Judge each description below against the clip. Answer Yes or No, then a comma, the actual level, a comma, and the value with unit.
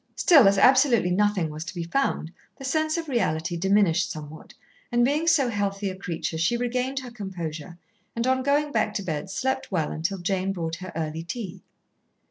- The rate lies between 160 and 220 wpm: Yes, average, 185 wpm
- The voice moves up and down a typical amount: No, wide, 6.9 semitones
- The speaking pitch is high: Yes, high, 195 Hz